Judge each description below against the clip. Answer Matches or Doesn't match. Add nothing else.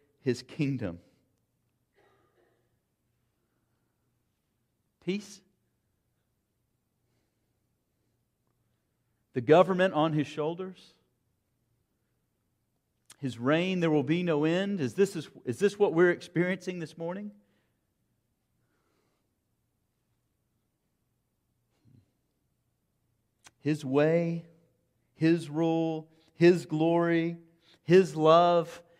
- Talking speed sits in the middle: Doesn't match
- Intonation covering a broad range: Matches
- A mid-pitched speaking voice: Matches